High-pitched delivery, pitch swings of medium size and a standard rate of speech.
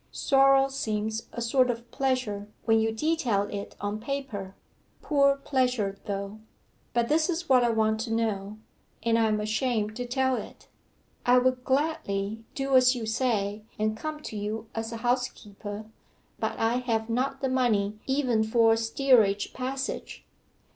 Yes: high, 230 Hz; average, 3.4 semitones; average, 160 wpm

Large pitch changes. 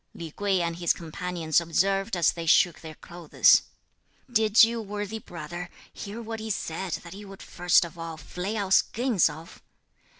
No: average, 3.5 semitones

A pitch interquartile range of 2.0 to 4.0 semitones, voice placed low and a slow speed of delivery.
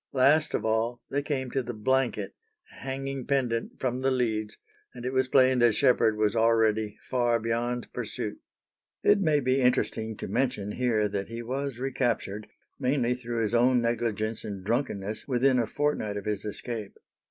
No: average, 3.1 semitones; low, 120 Hz; average, 165 wpm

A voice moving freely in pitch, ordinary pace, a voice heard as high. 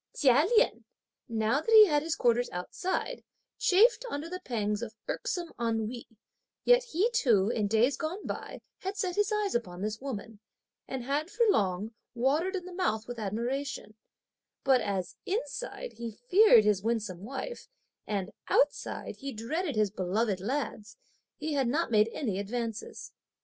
Yes: wide, 8.3 semitones; average, 155 wpm; high, 245 Hz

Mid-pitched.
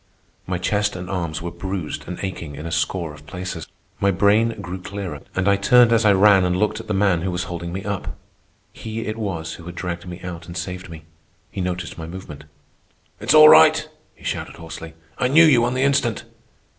No: very low, 95 Hz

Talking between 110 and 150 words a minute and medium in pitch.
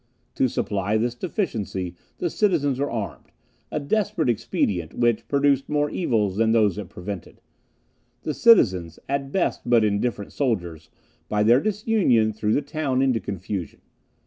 No: average, 145 wpm; low, 120 Hz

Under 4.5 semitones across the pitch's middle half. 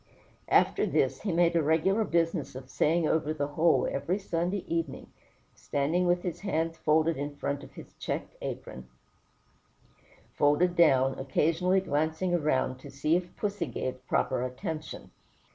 Yes: average, 3.5 semitones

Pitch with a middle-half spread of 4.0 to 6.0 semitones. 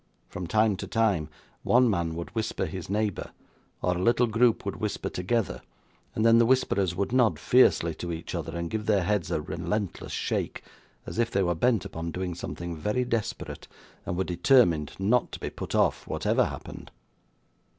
Yes: average, 4.8 semitones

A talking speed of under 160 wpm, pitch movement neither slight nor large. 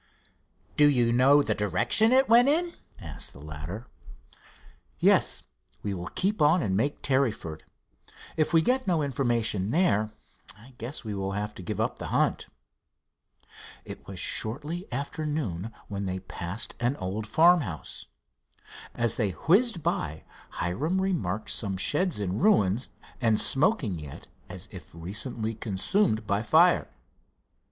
No: average, 140 wpm; wide, 8.3 semitones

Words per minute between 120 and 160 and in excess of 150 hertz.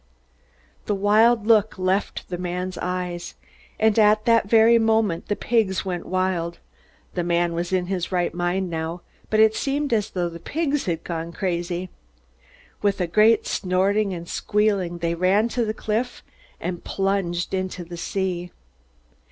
Yes: average, 155 wpm; medium, 185 Hz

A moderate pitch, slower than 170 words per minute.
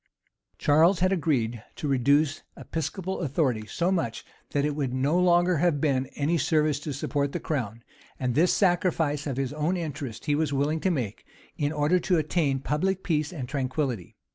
No: medium, 150 Hz; average, 180 wpm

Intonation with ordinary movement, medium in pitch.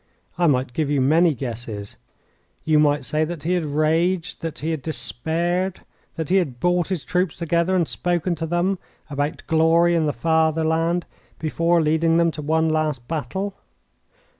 No: narrow, 2.3 semitones; medium, 160 Hz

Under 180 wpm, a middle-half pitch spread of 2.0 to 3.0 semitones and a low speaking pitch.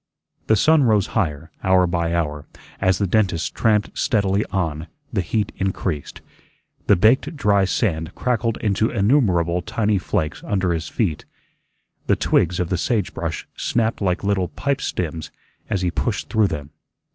No: average, 150 wpm; average, 4.2 semitones; very low, 95 Hz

